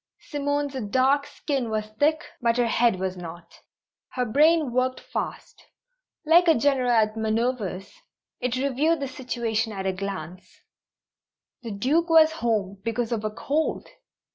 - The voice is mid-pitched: No, high, 245 Hz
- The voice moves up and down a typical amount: Yes, average, 4.9 semitones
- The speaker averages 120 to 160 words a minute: Yes, average, 145 wpm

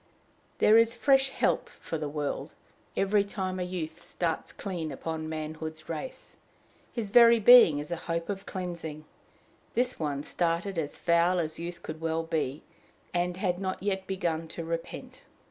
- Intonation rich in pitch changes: No, average, 3.4 semitones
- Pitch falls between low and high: Yes, medium, 170 Hz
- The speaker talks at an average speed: Yes, average, 160 wpm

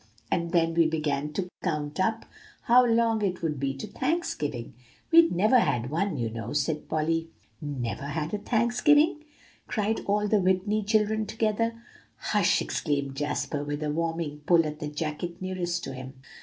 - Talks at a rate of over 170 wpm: No, average, 165 wpm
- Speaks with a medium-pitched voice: Yes, medium, 170 Hz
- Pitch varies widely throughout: Yes, wide, 6.4 semitones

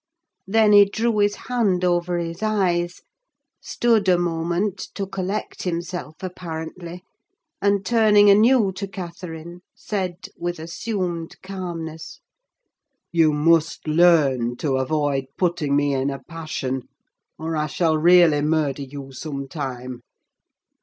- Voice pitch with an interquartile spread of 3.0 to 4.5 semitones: Yes, average, 3.8 semitones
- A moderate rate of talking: No, slow, 120 wpm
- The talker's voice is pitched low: No, medium, 170 Hz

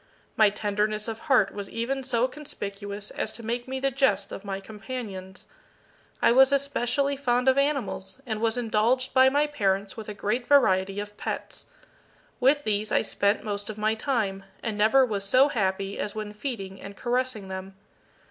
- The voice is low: No, high, 220 Hz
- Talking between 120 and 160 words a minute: No, average, 175 wpm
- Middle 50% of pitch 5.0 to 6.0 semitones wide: No, average, 4.3 semitones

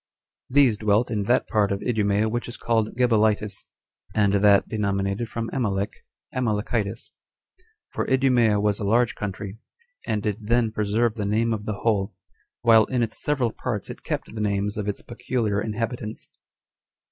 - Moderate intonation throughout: No, narrow, 2.3 semitones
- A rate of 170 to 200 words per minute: No, average, 160 wpm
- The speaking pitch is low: Yes, low, 110 Hz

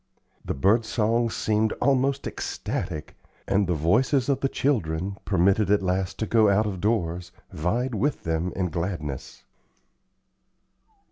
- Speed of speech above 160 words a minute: No, slow, 135 wpm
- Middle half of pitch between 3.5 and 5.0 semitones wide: Yes, average, 4.6 semitones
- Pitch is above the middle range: No, low, 100 Hz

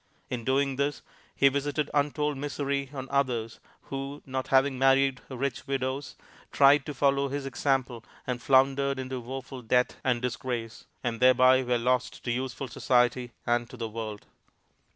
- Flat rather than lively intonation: Yes, narrow, 1.9 semitones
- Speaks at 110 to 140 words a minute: No, average, 150 wpm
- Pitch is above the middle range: No, low, 130 Hz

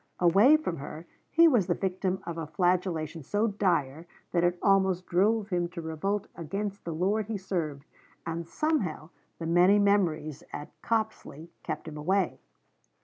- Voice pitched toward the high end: No, medium, 180 Hz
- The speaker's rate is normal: Yes, average, 155 wpm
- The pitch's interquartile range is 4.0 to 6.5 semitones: No, average, 3.6 semitones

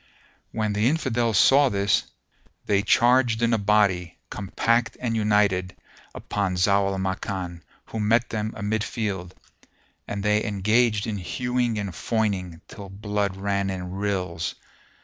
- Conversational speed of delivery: No, slow, 130 wpm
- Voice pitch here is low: Yes, low, 105 Hz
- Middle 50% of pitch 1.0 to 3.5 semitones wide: Yes, average, 2.7 semitones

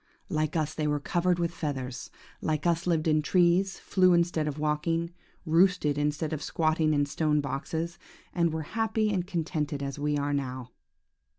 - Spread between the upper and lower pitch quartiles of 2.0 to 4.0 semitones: Yes, average, 2.7 semitones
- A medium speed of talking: Yes, average, 170 wpm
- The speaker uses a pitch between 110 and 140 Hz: No, medium, 155 Hz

